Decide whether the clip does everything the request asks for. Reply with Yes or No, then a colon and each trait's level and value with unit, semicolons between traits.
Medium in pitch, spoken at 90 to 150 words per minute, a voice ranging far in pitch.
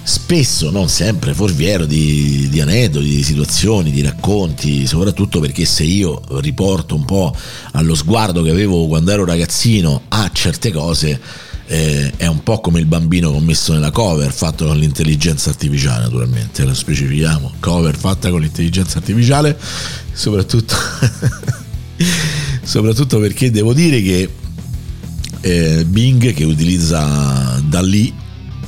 No: very low, 85 Hz; average, 135 wpm; wide, 5.9 semitones